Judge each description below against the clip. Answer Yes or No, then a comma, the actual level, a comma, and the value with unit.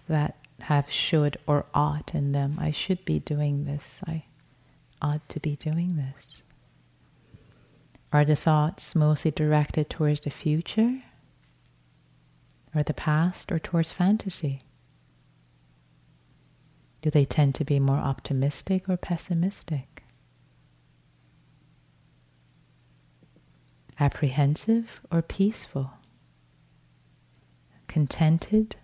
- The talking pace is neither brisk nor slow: No, slow, 95 wpm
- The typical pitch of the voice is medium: Yes, medium, 145 Hz